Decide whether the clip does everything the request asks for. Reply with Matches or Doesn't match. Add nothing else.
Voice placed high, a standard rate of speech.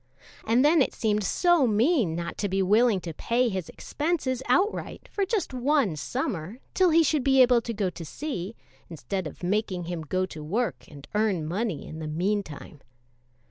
Matches